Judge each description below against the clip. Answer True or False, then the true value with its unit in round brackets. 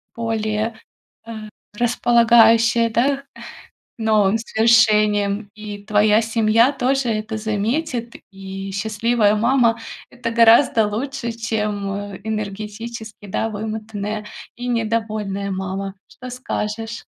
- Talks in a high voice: True (220 Hz)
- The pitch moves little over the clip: True (1.8 semitones)